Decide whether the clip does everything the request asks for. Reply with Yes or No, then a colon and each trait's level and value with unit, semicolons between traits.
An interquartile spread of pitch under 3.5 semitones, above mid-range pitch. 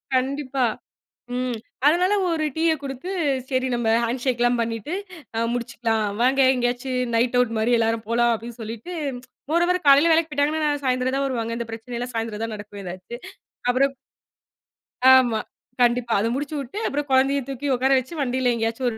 Yes: average, 3.1 semitones; very high, 250 Hz